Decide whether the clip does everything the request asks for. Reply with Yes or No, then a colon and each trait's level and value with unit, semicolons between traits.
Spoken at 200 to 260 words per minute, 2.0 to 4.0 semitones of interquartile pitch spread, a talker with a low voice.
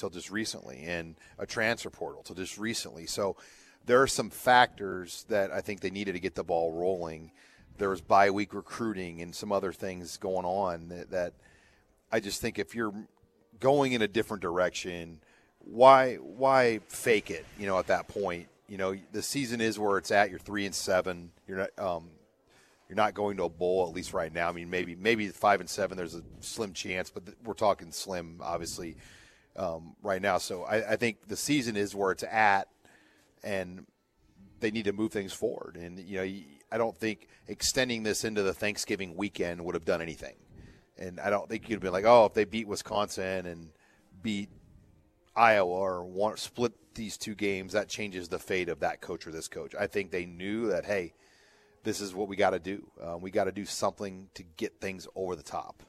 Yes: fast, 205 wpm; average, 3.5 semitones; low, 100 Hz